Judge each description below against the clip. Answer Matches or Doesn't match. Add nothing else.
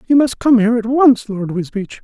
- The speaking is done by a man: Matches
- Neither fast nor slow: Doesn't match